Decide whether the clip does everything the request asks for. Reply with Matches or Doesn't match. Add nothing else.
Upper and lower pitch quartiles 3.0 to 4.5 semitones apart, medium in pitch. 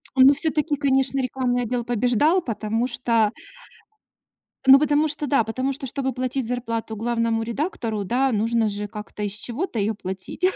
Doesn't match